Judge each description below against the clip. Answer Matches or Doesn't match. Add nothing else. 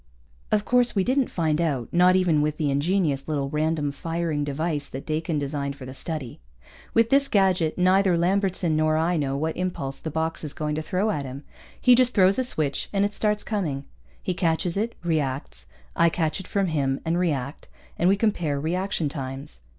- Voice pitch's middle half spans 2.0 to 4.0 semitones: Doesn't match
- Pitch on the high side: Doesn't match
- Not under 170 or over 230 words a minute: Matches